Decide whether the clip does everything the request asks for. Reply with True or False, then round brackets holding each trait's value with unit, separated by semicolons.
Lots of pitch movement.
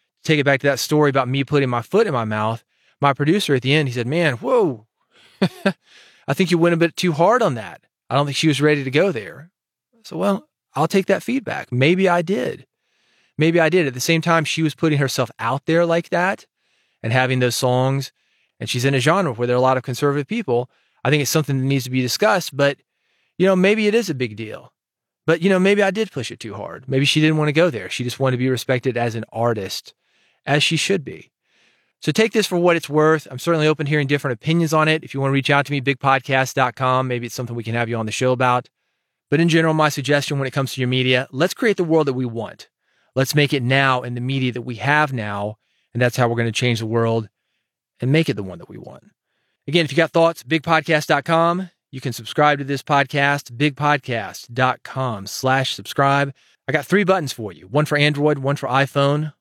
False (4.0 semitones)